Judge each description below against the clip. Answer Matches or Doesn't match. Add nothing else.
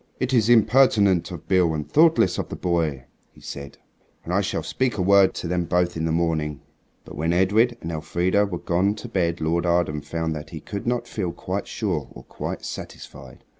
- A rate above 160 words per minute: Matches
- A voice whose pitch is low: Matches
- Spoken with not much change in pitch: Doesn't match